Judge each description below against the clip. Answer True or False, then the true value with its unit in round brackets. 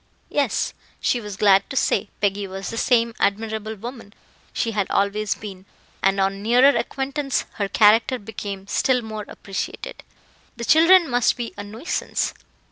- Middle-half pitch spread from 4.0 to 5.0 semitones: False (3.5 semitones)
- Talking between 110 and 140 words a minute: False (150 wpm)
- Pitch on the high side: True (220 Hz)